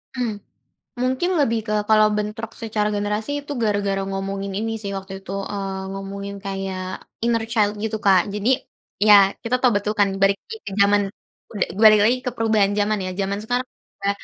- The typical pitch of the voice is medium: No, high, 210 Hz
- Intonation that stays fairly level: Yes, narrow, 2.1 semitones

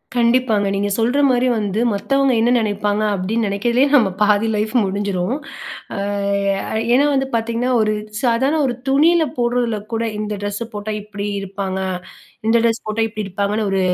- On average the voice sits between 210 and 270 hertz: Yes, high, 220 Hz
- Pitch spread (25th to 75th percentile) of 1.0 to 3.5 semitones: Yes, average, 3.0 semitones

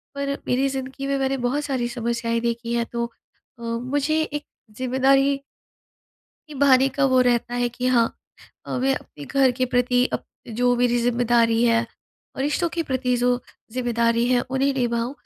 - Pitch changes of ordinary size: No, narrow, 2.3 semitones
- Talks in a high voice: Yes, very high, 250 Hz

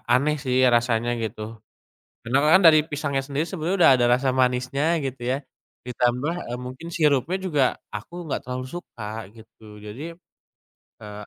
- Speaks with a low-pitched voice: Yes, low, 130 Hz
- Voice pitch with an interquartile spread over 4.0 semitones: No, average, 3.6 semitones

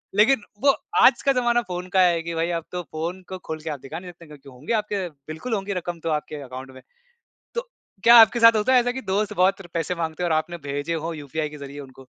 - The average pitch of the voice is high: No, medium, 170 Hz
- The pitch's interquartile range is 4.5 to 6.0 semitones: Yes, average, 5.1 semitones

